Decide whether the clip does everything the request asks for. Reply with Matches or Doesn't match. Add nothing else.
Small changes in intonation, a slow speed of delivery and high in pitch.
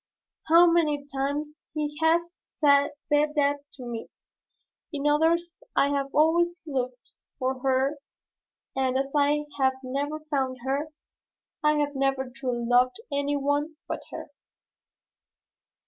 Matches